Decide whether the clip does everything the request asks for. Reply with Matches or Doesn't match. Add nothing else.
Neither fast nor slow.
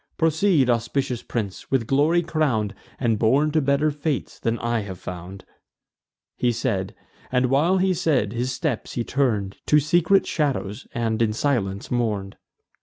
Matches